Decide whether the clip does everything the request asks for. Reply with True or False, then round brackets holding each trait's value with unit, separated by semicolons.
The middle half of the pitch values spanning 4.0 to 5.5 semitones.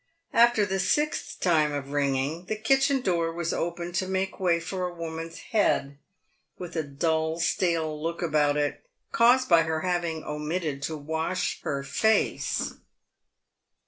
False (3.3 semitones)